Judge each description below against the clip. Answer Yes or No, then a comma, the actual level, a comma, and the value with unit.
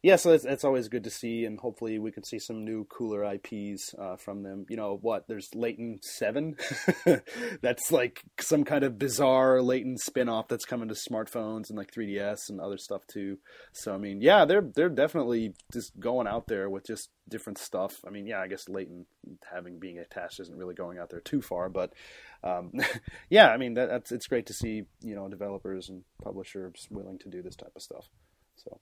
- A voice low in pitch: Yes, low, 110 Hz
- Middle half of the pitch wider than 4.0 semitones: No, average, 3.4 semitones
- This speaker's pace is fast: Yes, fast, 215 wpm